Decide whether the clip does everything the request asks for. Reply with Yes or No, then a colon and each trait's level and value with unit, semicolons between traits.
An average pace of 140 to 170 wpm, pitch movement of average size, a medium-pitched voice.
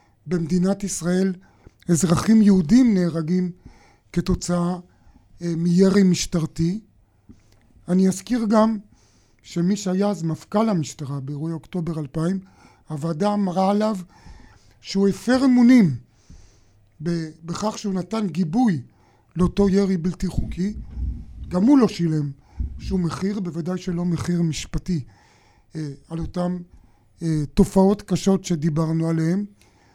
No: slow, 100 wpm; average, 4.6 semitones; medium, 175 Hz